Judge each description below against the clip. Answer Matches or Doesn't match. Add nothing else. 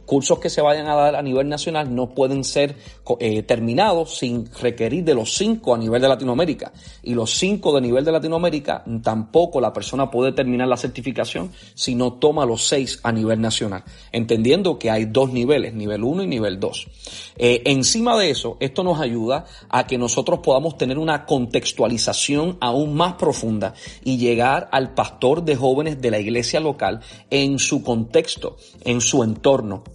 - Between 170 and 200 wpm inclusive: Matches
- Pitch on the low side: Matches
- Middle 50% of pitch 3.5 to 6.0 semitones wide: Matches